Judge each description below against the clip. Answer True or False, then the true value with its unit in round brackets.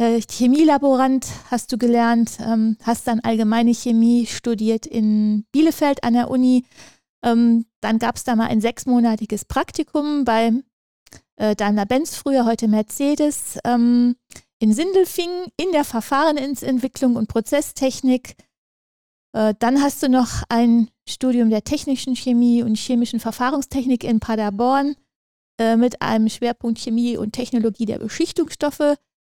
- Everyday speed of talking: False (115 wpm)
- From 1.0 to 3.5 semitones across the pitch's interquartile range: True (3.0 semitones)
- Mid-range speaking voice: False (240 Hz)